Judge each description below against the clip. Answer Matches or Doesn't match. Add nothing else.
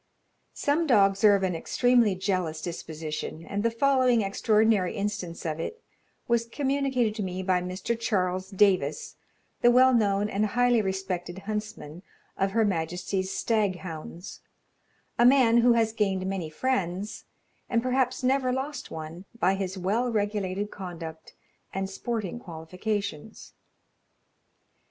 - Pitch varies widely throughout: Doesn't match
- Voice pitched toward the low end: Doesn't match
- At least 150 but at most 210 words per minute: Doesn't match